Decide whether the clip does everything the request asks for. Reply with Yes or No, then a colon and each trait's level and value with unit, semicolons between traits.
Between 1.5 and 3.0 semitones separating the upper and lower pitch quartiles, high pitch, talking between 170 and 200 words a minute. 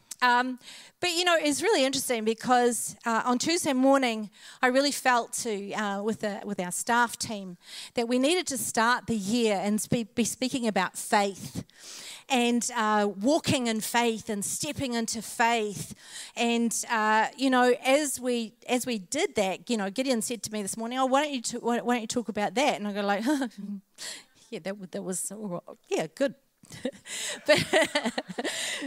No: average, 3.5 semitones; high, 235 Hz; average, 175 wpm